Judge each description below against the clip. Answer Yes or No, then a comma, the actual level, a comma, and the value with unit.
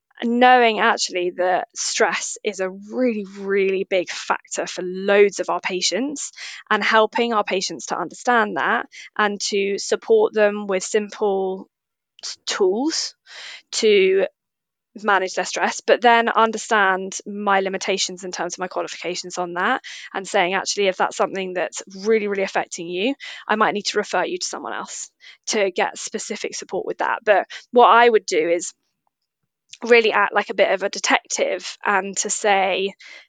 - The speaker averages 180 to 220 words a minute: No, average, 160 wpm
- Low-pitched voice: No, high, 200 Hz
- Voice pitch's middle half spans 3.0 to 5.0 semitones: Yes, average, 3.5 semitones